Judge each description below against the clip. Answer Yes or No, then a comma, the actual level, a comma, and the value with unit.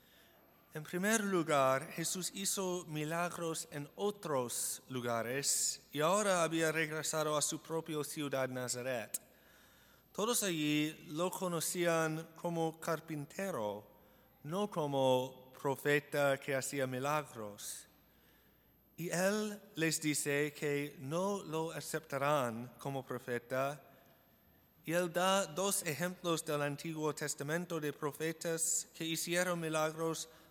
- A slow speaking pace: Yes, slow, 105 wpm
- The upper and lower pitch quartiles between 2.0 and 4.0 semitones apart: Yes, average, 3.4 semitones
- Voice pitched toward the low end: No, medium, 155 Hz